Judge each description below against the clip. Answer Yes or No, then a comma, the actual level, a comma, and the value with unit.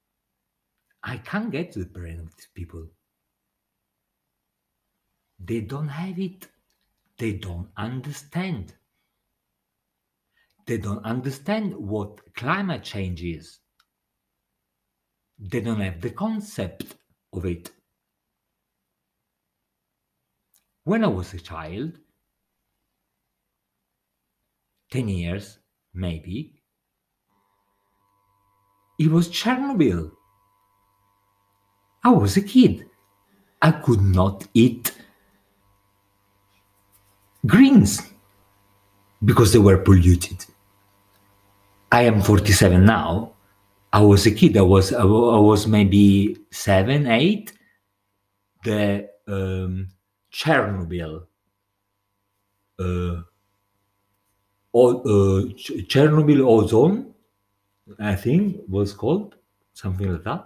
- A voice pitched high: No, low, 100 Hz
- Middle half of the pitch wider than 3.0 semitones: No, narrow, 2.6 semitones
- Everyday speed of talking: No, slow, 85 wpm